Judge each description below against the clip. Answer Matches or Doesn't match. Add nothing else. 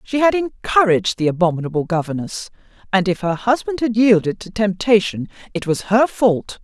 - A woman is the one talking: Matches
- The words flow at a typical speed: Matches